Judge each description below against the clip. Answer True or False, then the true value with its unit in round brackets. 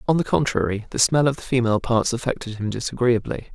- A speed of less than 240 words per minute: True (205 wpm)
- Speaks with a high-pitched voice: False (120 Hz)